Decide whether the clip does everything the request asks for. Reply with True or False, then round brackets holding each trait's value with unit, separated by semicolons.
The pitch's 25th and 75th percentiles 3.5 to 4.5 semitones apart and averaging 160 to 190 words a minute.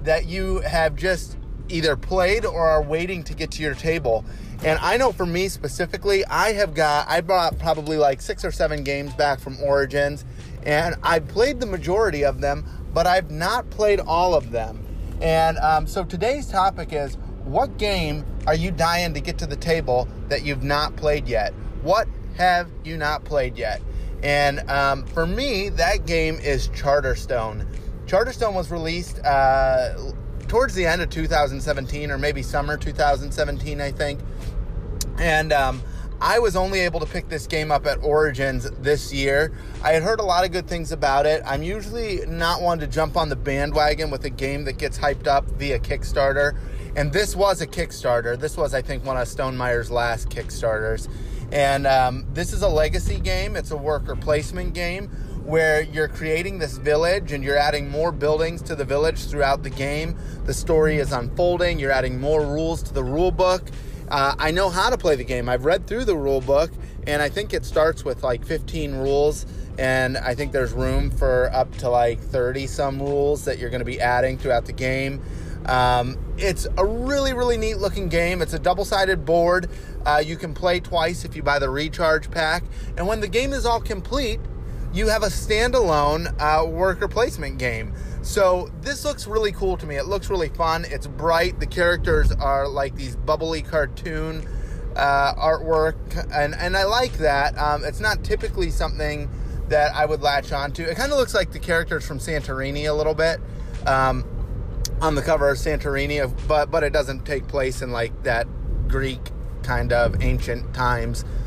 True (3.8 semitones; 185 wpm)